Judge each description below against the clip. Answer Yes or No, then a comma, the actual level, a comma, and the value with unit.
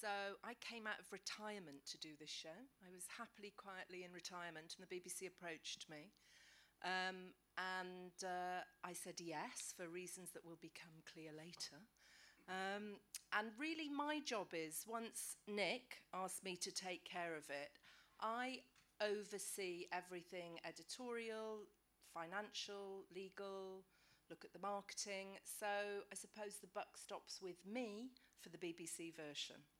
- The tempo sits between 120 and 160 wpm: Yes, average, 145 wpm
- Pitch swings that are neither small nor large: Yes, average, 3.2 semitones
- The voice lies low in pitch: No, medium, 185 Hz